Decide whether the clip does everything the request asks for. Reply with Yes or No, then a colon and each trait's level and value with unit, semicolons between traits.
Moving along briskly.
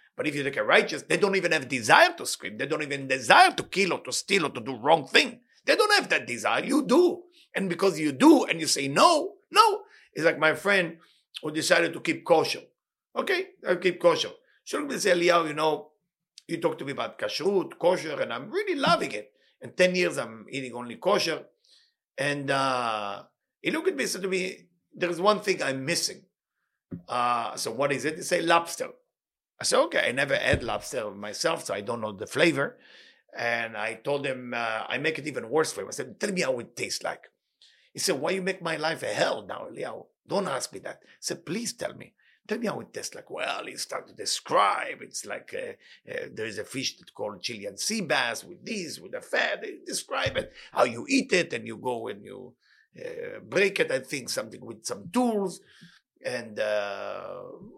Yes: fast, 215 wpm